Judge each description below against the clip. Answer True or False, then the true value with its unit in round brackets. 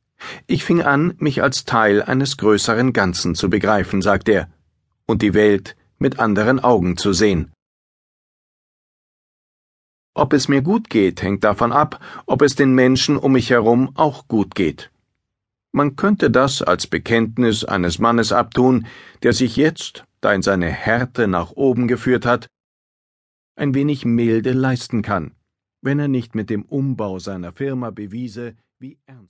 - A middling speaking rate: True (150 wpm)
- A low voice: True (115 Hz)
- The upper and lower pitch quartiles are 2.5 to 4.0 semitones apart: False (4.5 semitones)